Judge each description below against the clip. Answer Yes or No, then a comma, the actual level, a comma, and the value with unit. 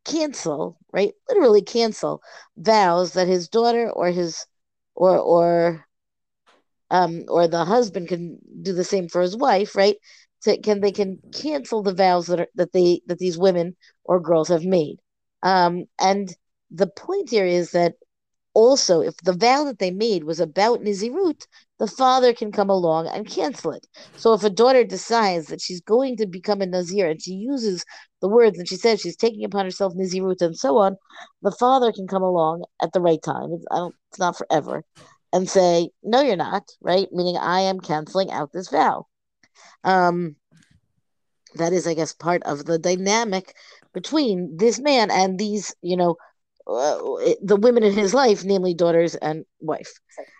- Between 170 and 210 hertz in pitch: Yes, high, 190 Hz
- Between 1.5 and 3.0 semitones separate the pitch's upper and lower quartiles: No, average, 3.9 semitones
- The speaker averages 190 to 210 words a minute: No, average, 175 wpm